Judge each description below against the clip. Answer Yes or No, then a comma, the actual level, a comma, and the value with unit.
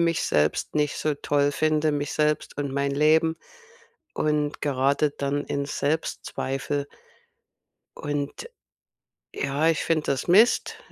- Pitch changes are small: Yes, narrow, 1.6 semitones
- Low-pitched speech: No, medium, 145 Hz